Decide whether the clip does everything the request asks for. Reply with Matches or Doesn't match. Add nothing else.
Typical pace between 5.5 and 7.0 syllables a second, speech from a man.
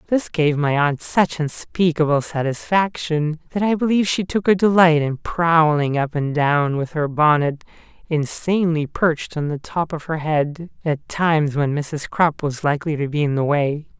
Doesn't match